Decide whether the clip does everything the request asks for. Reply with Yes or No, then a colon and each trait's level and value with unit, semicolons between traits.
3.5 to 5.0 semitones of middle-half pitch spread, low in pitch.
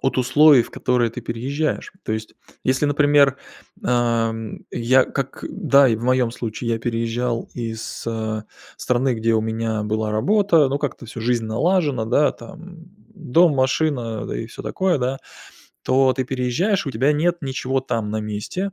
Yes: average, 4.1 semitones; low, 125 Hz